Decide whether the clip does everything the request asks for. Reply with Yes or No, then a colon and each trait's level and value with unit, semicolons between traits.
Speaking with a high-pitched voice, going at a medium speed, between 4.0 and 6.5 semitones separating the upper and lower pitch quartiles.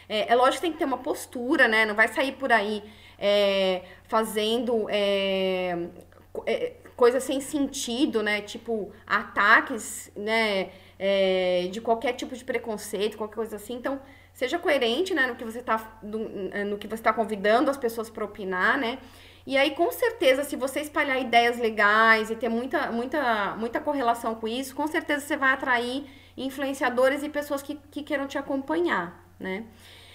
Yes: high, 235 Hz; average, 165 wpm; average, 4.6 semitones